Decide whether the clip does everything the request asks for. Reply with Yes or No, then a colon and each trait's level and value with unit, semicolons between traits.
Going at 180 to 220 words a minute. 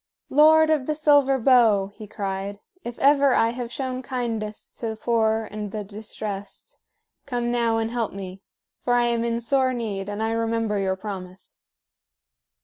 No: average, 165 wpm